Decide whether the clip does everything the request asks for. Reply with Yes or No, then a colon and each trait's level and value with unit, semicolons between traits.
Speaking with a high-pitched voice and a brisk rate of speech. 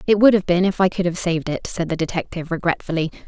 No: medium, 175 Hz; fast, 255 wpm